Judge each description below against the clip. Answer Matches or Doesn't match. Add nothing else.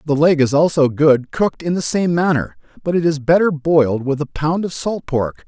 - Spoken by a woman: Doesn't match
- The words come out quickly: Matches